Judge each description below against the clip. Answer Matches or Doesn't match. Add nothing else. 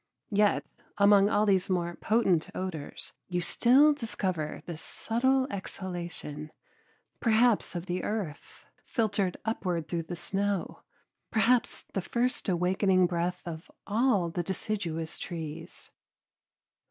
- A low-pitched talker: Doesn't match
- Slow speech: Matches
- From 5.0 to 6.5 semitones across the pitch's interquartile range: Doesn't match